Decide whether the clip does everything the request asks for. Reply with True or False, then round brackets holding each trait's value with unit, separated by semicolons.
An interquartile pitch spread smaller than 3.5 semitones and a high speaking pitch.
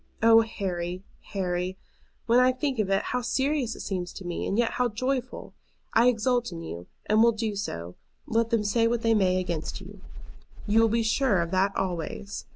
False (4.1 semitones; 215 Hz)